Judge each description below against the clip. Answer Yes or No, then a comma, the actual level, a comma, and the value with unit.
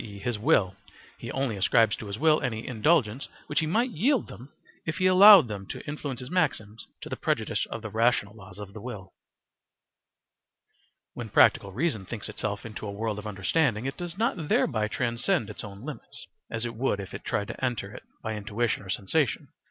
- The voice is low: Yes, low, 115 Hz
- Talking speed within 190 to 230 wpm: Yes, average, 200 wpm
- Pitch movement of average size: No, wide, 6.1 semitones